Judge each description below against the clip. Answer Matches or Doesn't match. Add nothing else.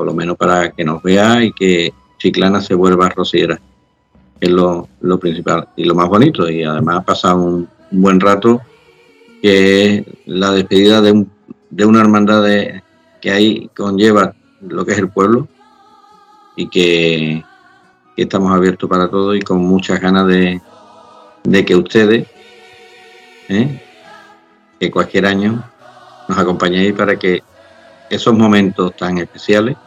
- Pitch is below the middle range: Matches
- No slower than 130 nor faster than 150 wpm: Matches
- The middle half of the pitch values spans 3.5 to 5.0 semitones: Doesn't match